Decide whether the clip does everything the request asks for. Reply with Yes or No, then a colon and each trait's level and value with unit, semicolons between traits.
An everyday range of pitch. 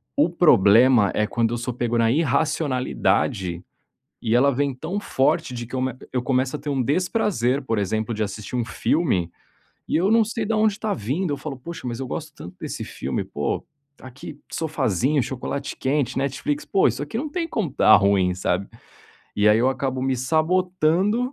No: wide, 5.7 semitones